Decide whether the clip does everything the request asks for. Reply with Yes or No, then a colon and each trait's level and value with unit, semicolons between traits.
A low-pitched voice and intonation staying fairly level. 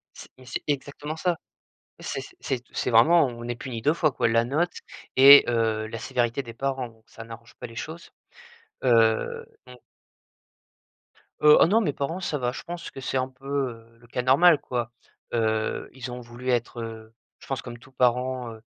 No: low, 125 Hz; average, 3.2 semitones